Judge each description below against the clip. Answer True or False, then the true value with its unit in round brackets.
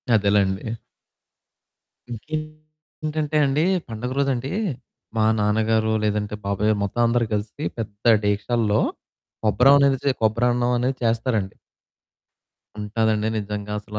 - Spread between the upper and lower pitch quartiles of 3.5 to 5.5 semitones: True (4.0 semitones)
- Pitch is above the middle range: False (110 Hz)